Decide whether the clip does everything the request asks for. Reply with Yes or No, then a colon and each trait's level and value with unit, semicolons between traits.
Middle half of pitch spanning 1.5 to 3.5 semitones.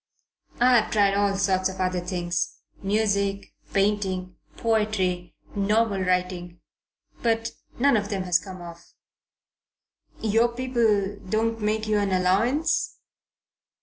Yes: average, 3.1 semitones